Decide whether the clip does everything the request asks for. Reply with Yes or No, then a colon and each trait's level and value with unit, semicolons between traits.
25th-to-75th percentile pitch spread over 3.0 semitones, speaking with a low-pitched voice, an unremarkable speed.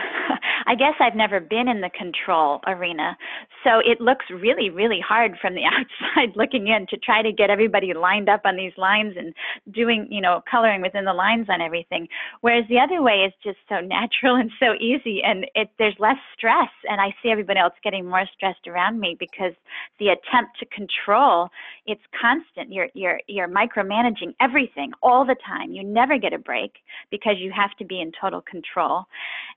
No: average, 3.7 semitones; high, 210 Hz; average, 190 wpm